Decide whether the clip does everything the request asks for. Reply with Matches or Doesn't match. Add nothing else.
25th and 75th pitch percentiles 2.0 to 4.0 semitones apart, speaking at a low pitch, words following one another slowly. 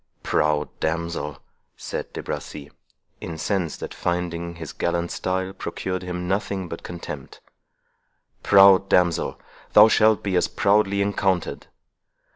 Matches